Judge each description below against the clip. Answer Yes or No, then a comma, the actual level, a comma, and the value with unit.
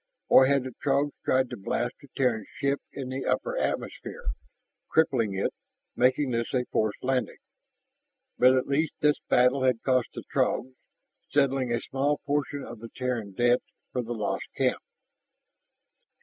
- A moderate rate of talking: Yes, average, 155 wpm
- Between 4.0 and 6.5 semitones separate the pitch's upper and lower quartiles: No, narrow, 2.4 semitones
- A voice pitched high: No, low, 130 Hz